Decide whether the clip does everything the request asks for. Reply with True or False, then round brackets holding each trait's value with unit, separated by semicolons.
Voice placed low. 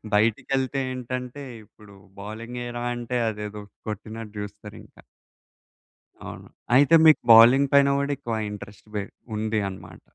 True (115 Hz)